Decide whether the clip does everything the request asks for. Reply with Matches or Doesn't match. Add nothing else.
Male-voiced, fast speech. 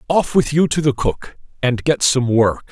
Matches